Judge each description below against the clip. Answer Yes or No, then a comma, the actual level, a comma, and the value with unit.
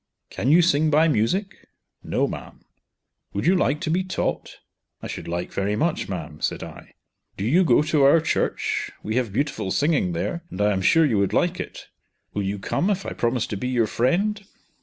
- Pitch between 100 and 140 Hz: Yes, low, 135 Hz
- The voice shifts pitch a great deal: Yes, wide, 8.3 semitones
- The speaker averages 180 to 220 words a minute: Yes, average, 200 wpm